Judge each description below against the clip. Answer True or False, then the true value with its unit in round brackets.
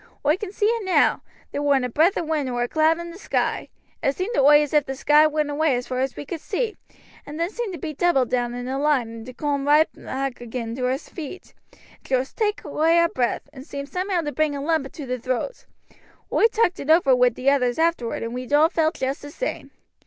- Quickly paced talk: True (250 wpm)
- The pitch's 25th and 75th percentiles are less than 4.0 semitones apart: False (4.3 semitones)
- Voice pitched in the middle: False (290 Hz)